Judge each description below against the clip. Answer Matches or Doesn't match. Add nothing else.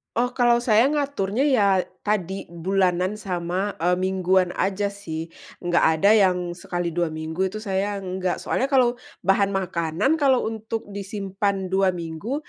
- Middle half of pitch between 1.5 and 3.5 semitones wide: Matches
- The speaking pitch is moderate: Doesn't match